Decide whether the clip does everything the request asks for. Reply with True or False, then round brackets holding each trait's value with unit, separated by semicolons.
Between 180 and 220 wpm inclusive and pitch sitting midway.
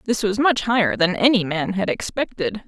False (200 wpm; 215 Hz)